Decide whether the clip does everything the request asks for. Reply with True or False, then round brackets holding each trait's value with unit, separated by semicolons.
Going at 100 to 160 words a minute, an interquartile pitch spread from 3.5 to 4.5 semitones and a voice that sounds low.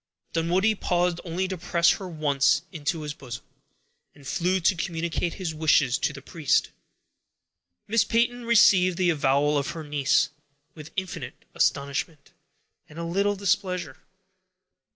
False (135 wpm; 4.0 semitones; 170 Hz)